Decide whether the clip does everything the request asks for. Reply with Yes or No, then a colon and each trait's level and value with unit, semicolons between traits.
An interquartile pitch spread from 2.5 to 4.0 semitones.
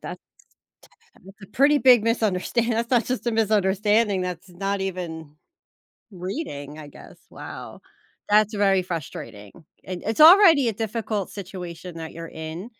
No: average, 4.6 semitones